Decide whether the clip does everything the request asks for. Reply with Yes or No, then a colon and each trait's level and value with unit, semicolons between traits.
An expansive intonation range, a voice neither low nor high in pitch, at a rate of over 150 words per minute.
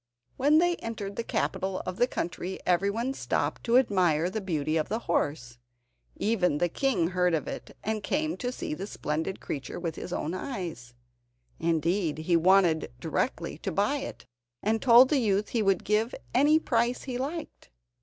No: wide, 6.0 semitones; high, 195 Hz; average, 175 wpm